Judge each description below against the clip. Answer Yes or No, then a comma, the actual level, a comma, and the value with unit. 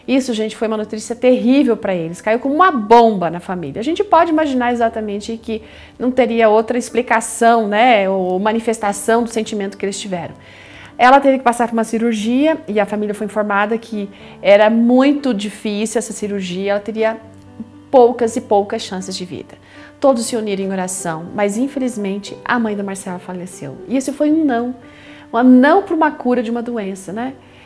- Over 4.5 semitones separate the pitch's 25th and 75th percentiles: No, average, 3.4 semitones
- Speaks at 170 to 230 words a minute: Yes, average, 180 wpm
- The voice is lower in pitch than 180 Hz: No, high, 225 Hz